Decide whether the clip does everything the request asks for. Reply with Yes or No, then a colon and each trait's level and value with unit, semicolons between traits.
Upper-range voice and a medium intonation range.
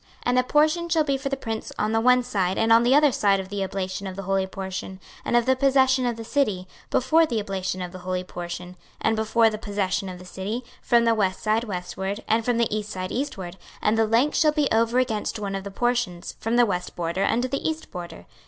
Yes: high, 220 Hz; average, 4.6 semitones